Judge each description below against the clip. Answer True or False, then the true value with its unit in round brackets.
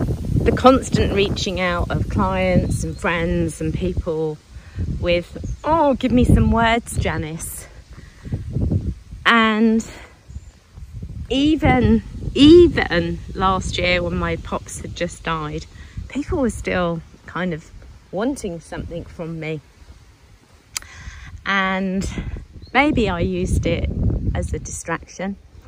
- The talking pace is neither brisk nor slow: False (105 wpm)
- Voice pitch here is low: False (165 Hz)